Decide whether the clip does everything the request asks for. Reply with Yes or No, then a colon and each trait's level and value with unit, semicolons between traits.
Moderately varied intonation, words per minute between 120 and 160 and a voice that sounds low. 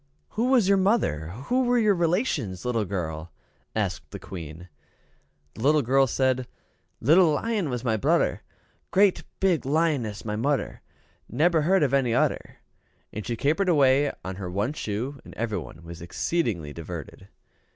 No: wide, 8.9 semitones; average, 150 wpm; low, 130 Hz